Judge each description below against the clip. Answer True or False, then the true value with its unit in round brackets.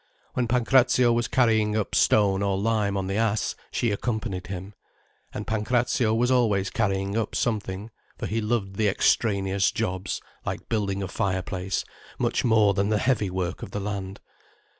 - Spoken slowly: False (165 wpm)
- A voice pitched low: True (105 Hz)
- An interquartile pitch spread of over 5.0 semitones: False (2.7 semitones)